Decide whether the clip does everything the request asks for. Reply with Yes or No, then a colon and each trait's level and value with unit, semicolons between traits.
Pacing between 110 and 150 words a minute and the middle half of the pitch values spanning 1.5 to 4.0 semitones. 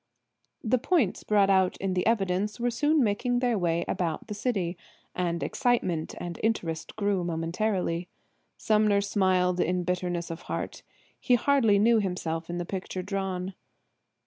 Yes: average, 145 wpm; average, 3.6 semitones